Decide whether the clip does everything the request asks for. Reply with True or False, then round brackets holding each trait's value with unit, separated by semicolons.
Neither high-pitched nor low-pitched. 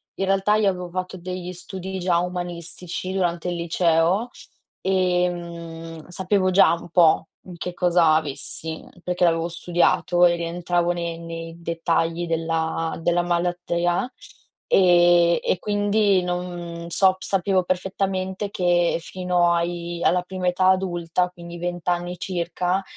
True (175 Hz)